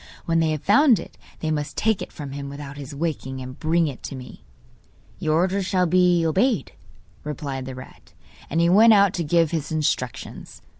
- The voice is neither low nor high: Yes, medium, 160 Hz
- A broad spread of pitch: No, average, 4.2 semitones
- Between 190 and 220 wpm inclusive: Yes, average, 195 wpm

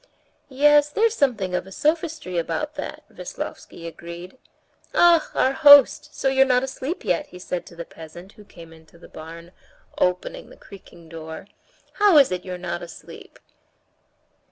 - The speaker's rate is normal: Yes, average, 155 wpm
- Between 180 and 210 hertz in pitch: Yes, medium, 185 Hz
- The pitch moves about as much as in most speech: No, wide, 8.9 semitones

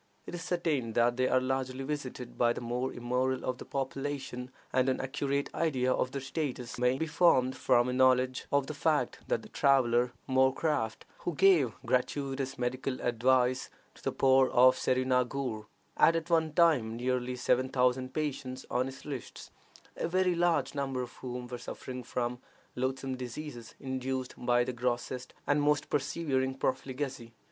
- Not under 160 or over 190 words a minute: Yes, average, 165 wpm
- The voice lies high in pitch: No, low, 130 Hz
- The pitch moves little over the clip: Yes, narrow, 1.9 semitones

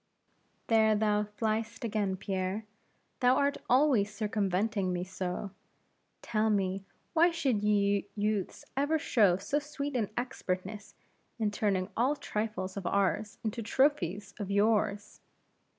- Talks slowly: Yes, slow, 125 wpm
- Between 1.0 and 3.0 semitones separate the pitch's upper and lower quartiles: Yes, narrow, 2.5 semitones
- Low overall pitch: No, high, 210 Hz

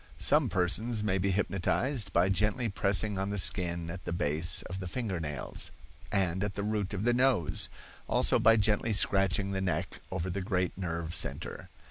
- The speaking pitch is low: Yes, very low, 95 Hz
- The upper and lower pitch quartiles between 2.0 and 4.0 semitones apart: Yes, average, 2.9 semitones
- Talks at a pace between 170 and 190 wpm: Yes, average, 180 wpm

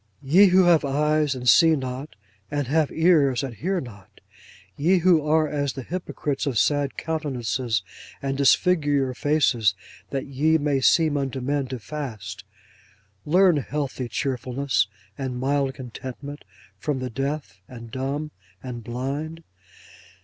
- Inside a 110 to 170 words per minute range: Yes, average, 140 wpm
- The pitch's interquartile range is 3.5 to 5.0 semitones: No, average, 3.0 semitones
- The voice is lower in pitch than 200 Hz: Yes, medium, 140 Hz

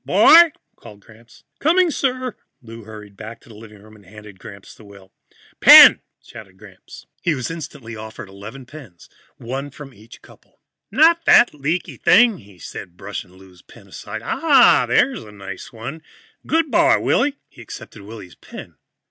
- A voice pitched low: Yes, low, 115 Hz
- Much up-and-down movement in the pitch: Yes, wide, 8.3 semitones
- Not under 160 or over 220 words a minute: Yes, average, 165 wpm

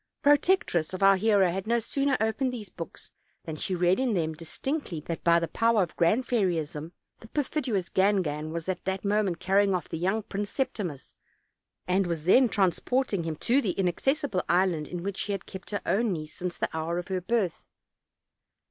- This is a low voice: No, high, 190 Hz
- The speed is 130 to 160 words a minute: No, average, 195 wpm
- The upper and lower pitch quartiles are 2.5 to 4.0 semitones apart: No, average, 4.5 semitones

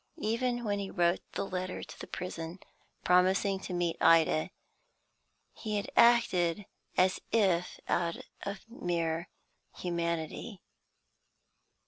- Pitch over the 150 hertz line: Yes, medium, 185 Hz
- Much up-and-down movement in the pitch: No, average, 3.1 semitones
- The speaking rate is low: Yes, slow, 110 wpm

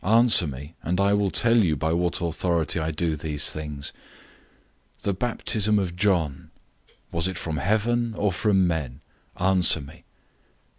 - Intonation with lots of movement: No, average, 4.5 semitones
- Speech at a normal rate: Yes, average, 155 wpm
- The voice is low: Yes, very low, 90 Hz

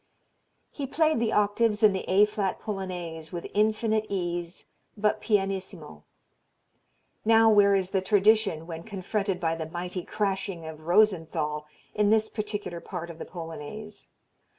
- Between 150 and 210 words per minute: No, average, 140 wpm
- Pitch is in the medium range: No, high, 195 Hz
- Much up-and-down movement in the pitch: No, average, 3.8 semitones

